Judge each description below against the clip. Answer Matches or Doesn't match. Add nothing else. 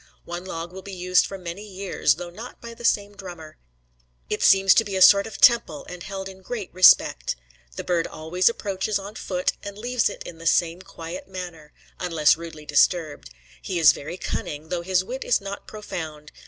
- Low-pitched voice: Doesn't match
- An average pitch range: Matches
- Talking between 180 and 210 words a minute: Matches